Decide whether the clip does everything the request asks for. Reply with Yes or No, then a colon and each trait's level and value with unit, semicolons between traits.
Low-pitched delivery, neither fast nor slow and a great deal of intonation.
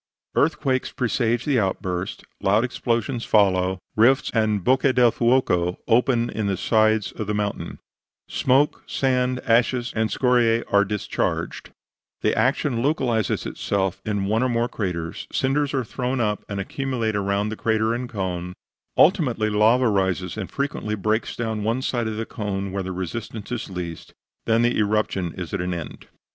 No: low, 110 Hz; average, 160 wpm; average, 3.9 semitones